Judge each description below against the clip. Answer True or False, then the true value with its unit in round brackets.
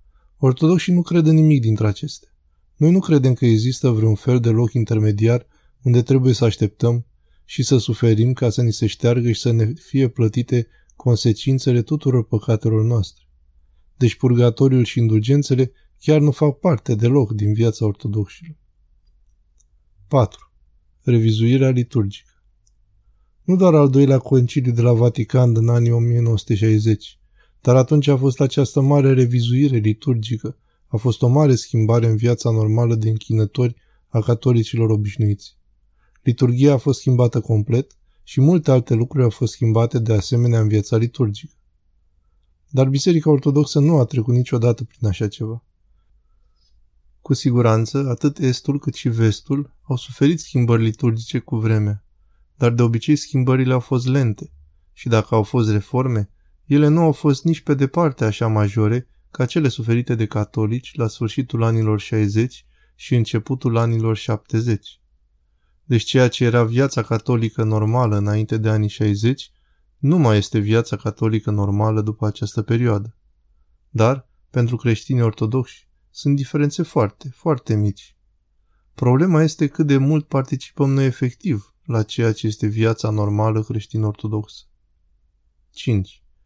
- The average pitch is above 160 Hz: False (115 Hz)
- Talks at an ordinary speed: True (140 wpm)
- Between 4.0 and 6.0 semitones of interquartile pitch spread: False (3.5 semitones)